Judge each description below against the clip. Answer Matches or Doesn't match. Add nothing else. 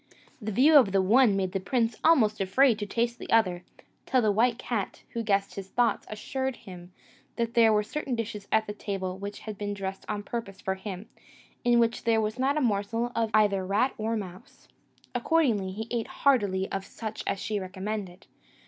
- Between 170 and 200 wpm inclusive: Matches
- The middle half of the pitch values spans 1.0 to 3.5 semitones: Matches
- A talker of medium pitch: Doesn't match